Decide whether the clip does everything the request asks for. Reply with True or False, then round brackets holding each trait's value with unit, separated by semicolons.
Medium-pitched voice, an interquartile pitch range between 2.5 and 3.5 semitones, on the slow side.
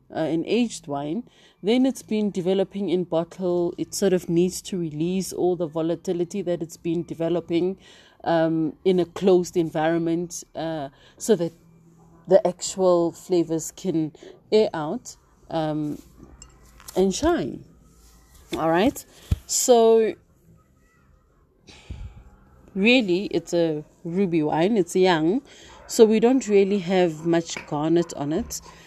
True (170 Hz; 2.8 semitones; 125 wpm)